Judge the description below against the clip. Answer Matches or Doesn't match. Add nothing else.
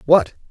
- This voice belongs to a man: Matches